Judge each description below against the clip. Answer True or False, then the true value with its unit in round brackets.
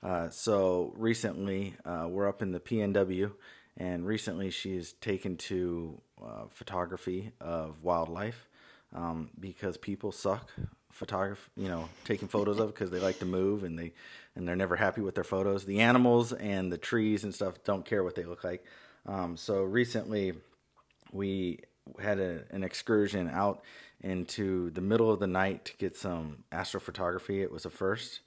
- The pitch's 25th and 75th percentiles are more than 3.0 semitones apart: False (2.6 semitones)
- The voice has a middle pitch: False (95 Hz)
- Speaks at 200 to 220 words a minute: False (165 wpm)